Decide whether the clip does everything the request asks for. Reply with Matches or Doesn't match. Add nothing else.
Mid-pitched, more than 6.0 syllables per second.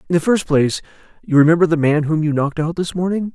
Matches